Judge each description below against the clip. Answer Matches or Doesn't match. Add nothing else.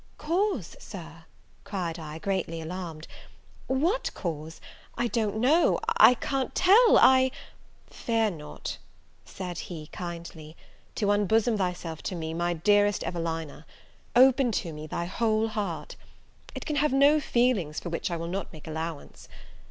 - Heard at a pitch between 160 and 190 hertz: Matches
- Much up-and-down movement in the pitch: Matches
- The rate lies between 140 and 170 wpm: Matches